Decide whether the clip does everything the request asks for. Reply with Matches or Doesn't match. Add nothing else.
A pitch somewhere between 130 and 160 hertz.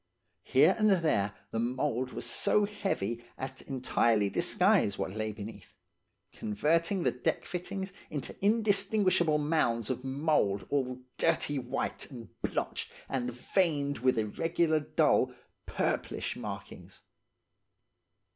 Matches